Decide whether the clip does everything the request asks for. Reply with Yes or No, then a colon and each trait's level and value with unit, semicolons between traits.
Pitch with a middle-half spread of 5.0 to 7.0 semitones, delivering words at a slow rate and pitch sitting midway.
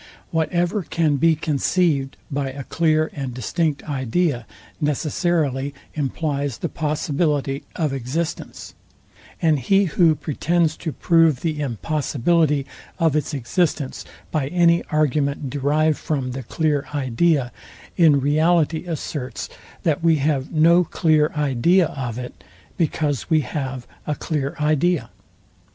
No: average, 3.1 semitones; slow, 120 wpm; medium, 150 Hz